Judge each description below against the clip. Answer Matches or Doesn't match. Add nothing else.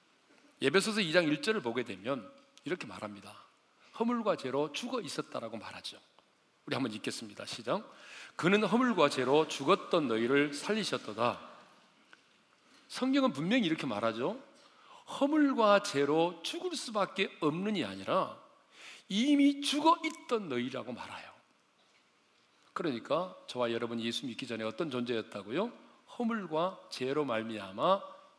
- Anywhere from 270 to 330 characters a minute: Matches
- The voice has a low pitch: Doesn't match